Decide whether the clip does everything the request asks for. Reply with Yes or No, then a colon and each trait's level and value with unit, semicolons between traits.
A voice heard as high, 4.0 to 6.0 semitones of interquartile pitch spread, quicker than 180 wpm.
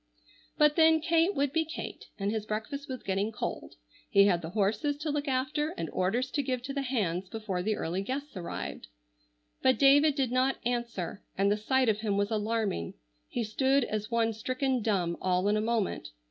Yes: high, 230 Hz; average, 5.3 semitones; average, 195 wpm